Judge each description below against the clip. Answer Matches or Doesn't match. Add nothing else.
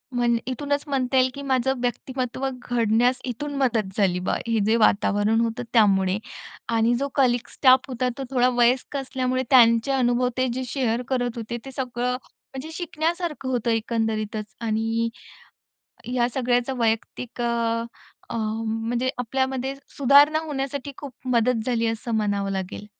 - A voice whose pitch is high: Matches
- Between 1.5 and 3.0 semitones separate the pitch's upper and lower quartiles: Matches